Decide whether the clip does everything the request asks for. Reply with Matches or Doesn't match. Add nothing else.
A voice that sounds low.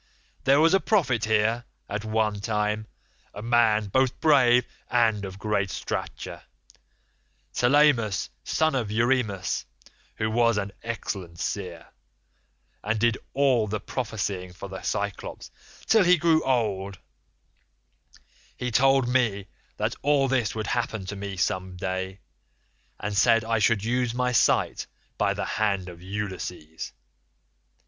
Matches